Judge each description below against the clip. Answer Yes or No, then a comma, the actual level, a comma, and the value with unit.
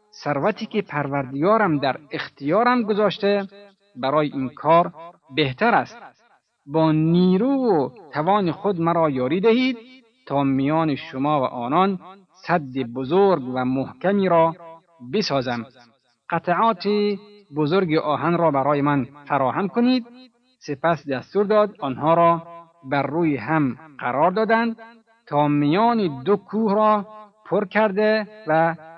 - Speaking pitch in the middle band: Yes, medium, 170 Hz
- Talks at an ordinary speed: Yes, average, 115 wpm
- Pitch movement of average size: No, wide, 6.0 semitones